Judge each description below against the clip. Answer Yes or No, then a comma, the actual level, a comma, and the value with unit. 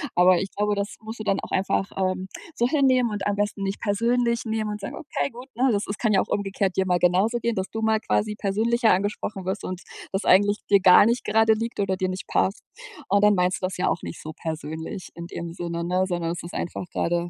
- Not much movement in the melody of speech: No, average, 3.0 semitones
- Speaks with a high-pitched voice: Yes, high, 200 Hz